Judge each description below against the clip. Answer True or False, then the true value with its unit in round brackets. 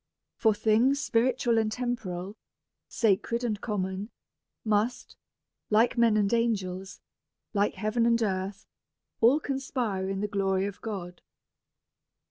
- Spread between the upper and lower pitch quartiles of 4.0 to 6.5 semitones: False (3.2 semitones)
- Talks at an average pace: False (120 wpm)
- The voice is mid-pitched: False (215 Hz)